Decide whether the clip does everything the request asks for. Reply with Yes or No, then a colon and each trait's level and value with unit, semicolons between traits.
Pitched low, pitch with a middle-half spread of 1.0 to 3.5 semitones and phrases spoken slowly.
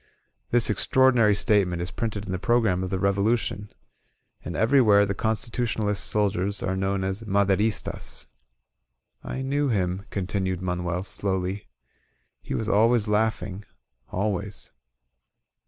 Yes: low, 100 Hz; average, 2.7 semitones; slow, 120 wpm